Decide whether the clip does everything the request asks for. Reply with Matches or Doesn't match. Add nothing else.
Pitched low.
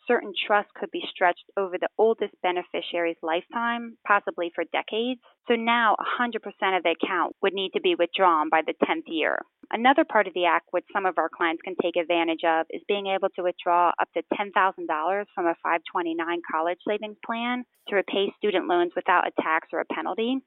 Doesn't match